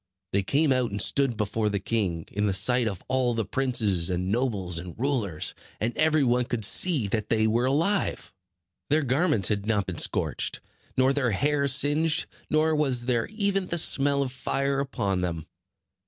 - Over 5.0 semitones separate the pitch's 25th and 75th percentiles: Yes, wide, 5.6 semitones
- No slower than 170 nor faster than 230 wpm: Yes, average, 180 wpm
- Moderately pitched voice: No, low, 125 Hz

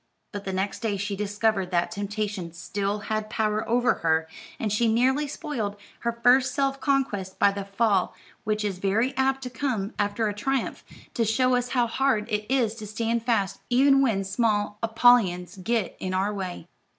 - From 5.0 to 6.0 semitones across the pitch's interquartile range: No, average, 3.6 semitones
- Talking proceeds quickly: No, average, 180 wpm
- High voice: Yes, high, 215 Hz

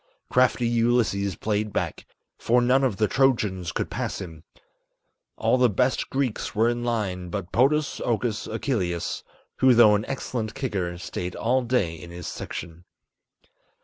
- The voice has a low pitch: Yes, low, 110 Hz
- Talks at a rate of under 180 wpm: Yes, average, 145 wpm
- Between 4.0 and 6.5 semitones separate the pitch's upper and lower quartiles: Yes, average, 5.0 semitones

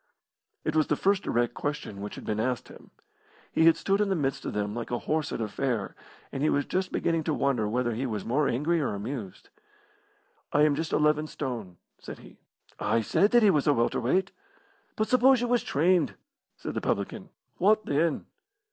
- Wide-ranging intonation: Yes, wide, 6.3 semitones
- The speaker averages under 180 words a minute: No, fast, 205 wpm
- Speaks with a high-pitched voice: No, medium, 145 Hz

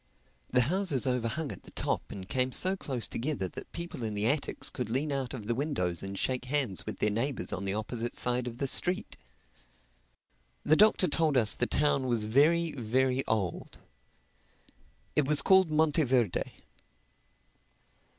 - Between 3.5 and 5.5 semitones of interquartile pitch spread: Yes, average, 4.7 semitones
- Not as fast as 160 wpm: No, average, 165 wpm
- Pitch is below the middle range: Yes, low, 130 Hz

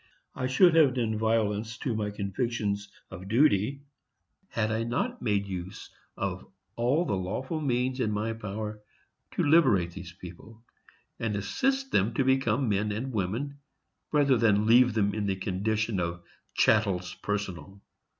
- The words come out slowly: No, average, 150 wpm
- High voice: No, low, 110 Hz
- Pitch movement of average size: Yes, average, 4.2 semitones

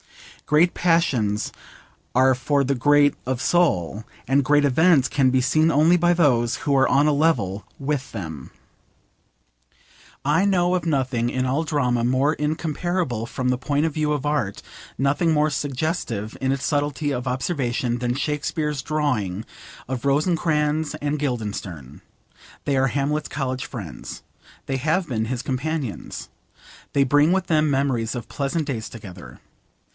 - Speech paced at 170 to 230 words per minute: No, average, 150 wpm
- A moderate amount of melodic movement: Yes, average, 3.5 semitones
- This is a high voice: No, medium, 140 Hz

